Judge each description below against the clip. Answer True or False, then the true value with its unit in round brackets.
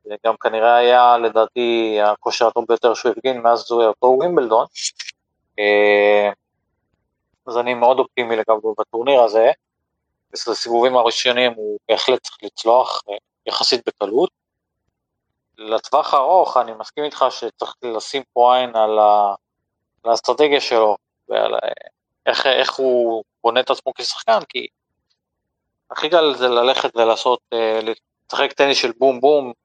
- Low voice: True (115 Hz)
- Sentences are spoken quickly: False (125 wpm)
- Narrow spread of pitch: True (2.2 semitones)